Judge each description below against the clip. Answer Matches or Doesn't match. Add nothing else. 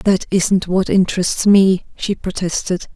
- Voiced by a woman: Matches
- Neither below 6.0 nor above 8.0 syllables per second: Doesn't match